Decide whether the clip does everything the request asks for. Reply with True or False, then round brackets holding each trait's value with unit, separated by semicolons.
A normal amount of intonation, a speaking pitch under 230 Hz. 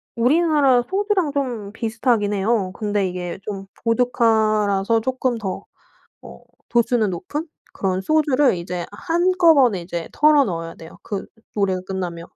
False (5.9 semitones; 220 Hz)